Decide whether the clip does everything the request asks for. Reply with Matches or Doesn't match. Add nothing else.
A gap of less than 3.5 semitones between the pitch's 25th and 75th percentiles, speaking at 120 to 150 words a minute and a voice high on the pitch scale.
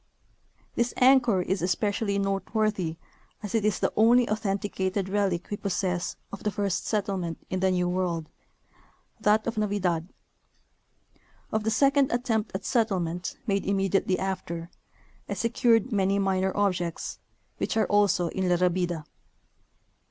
Matches